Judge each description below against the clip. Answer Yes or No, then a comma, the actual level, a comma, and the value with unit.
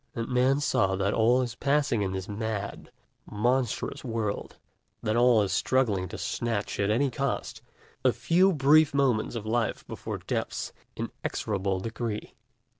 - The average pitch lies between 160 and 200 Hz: No, low, 115 Hz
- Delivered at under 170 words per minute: Yes, average, 145 wpm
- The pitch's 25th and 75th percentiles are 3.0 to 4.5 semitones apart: Yes, average, 4.2 semitones